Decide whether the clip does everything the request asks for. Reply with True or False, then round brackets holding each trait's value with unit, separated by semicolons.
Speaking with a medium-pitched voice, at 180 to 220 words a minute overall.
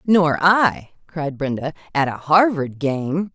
False (160 Hz; 145 wpm)